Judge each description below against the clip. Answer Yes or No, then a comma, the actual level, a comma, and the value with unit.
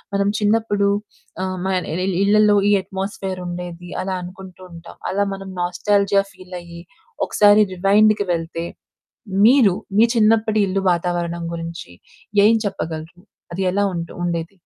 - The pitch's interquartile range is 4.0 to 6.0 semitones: No, average, 2.8 semitones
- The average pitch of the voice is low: No, high, 190 Hz